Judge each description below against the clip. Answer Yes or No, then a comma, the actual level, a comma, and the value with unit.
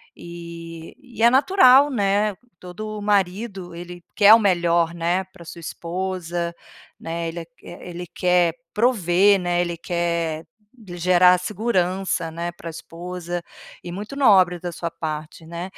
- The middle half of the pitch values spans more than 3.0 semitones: No, average, 2.7 semitones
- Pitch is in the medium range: Yes, medium, 175 Hz